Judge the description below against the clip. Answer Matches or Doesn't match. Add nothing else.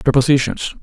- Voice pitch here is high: Doesn't match